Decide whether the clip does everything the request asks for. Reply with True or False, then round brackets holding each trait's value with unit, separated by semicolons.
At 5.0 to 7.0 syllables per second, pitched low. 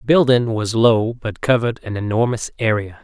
True (5.1 syllables/s; 115 Hz)